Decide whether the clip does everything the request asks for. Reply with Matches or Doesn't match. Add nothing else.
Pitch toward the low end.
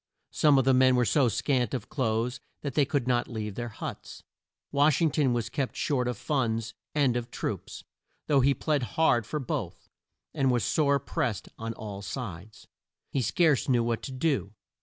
Matches